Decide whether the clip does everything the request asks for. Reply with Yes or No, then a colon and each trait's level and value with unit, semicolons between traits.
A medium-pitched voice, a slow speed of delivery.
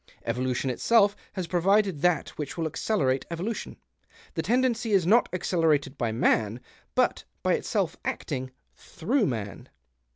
Yes: medium, 170 Hz; slow, 130 wpm